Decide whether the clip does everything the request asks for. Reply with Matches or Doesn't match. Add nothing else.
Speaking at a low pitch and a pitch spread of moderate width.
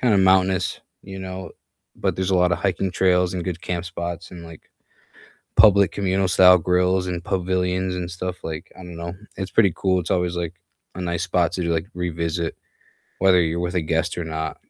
Doesn't match